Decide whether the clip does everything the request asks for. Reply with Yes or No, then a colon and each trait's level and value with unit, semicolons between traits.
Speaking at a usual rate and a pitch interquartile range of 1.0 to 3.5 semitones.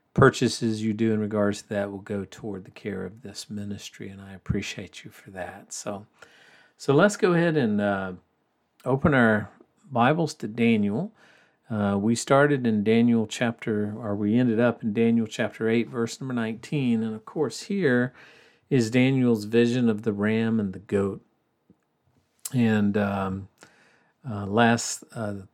Yes: average, 160 wpm; average, 3.1 semitones